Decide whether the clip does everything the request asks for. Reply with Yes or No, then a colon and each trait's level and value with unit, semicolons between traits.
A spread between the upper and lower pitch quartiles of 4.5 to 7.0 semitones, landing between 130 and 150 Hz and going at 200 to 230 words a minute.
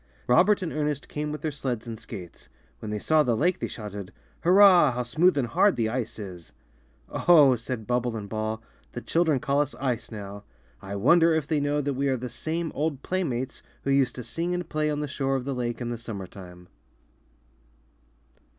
Yes: average, 5.2 semitones; low, 135 Hz; fast, 205 wpm